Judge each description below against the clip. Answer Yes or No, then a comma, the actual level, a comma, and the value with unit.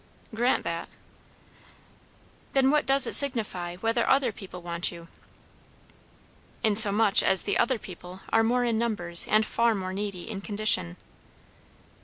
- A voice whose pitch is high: Yes, high, 215 Hz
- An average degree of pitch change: Yes, average, 4.4 semitones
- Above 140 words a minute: No, slow, 135 wpm